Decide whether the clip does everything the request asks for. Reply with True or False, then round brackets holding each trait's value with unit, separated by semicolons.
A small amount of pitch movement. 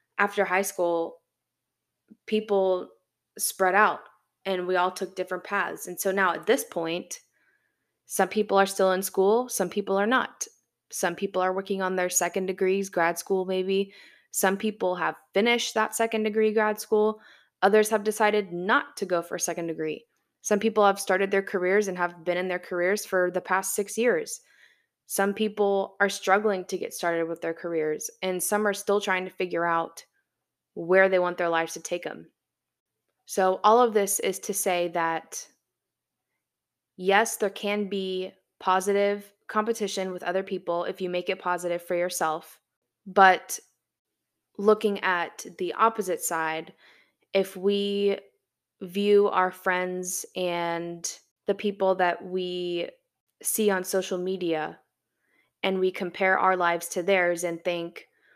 True (2.3 semitones)